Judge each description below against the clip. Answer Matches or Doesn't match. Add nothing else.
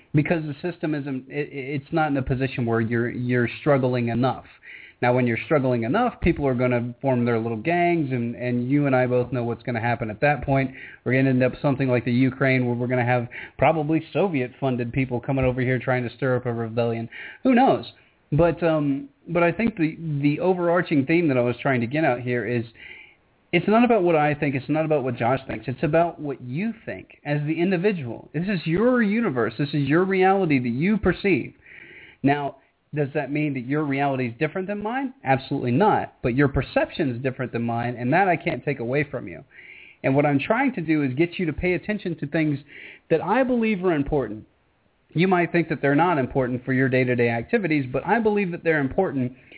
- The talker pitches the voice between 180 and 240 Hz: Doesn't match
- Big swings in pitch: Doesn't match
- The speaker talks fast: Matches